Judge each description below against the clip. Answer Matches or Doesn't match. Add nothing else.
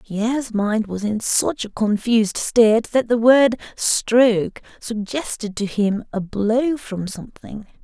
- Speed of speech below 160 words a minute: Matches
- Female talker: Matches